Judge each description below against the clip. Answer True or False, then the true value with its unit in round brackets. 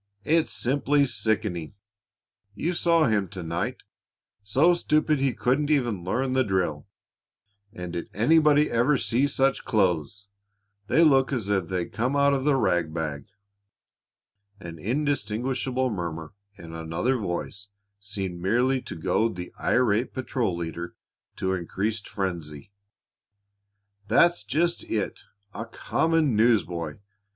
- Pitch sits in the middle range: False (110 Hz)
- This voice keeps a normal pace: False (125 wpm)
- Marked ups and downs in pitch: True (7.2 semitones)